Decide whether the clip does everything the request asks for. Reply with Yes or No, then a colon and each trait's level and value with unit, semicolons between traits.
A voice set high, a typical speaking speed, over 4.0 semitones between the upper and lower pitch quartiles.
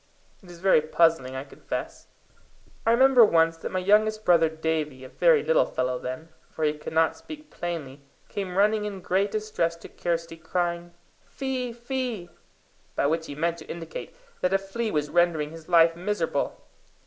No: medium, 170 Hz; average, 170 wpm; average, 4.6 semitones